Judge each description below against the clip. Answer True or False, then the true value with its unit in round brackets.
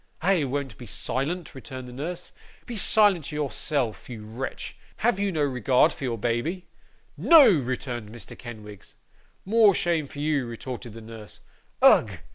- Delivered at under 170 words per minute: True (150 wpm)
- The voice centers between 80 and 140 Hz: True (135 Hz)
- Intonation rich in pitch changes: True (6.5 semitones)